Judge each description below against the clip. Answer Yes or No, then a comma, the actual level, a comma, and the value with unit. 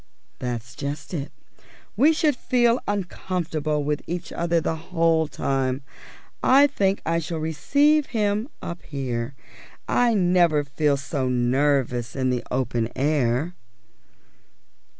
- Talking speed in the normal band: No, slow, 120 wpm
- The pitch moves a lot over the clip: Yes, wide, 5.7 semitones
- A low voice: No, medium, 155 Hz